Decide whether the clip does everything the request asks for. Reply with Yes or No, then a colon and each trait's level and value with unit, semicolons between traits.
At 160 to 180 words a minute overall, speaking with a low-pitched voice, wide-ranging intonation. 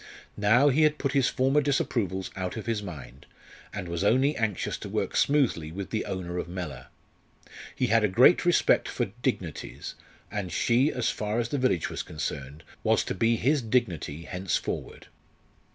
Yes: average, 170 wpm; low, 110 Hz; wide, 6.3 semitones